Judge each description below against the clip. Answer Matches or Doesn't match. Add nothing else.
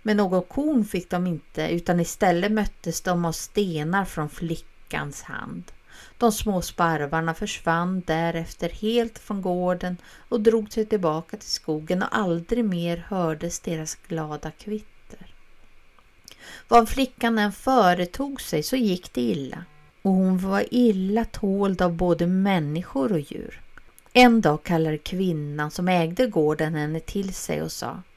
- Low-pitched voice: Doesn't match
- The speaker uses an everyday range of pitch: Matches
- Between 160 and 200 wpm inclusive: Doesn't match